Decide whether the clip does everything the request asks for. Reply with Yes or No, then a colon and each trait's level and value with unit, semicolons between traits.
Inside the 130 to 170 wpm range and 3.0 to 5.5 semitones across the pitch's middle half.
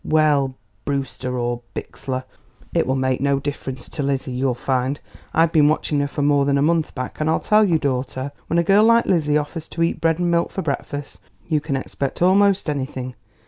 No: fast, 205 wpm; average, 3.6 semitones